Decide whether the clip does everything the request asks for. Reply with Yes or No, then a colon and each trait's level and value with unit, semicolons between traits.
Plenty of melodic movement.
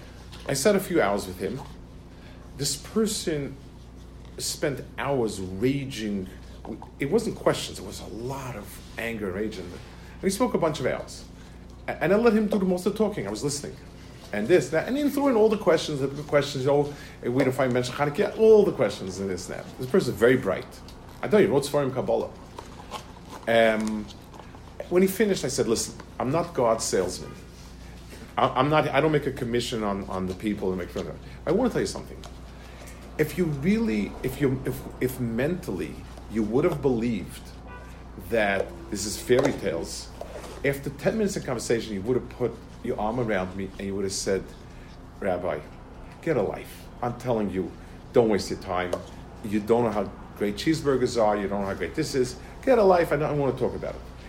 Yes: wide, 7.2 semitones